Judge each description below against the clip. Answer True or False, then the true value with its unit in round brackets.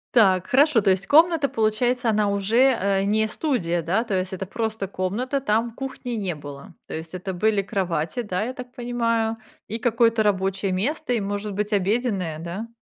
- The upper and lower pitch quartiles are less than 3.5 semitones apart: False (4.0 semitones)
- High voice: True (210 Hz)